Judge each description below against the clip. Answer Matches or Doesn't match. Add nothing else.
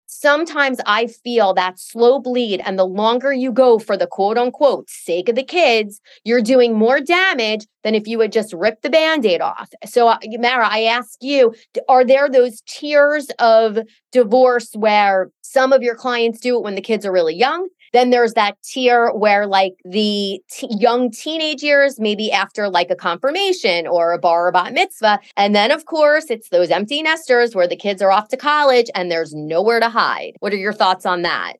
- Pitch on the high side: Matches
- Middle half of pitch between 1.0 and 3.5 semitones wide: Doesn't match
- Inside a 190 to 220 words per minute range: Matches